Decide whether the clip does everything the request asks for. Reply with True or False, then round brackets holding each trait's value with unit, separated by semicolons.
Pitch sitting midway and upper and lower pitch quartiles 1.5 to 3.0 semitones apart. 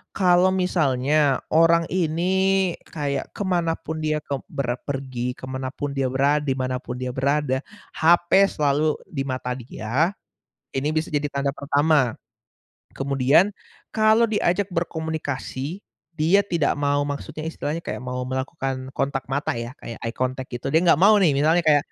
False (145 Hz; 4.1 semitones)